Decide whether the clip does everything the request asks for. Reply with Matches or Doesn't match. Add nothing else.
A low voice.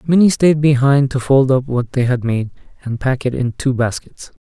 Matches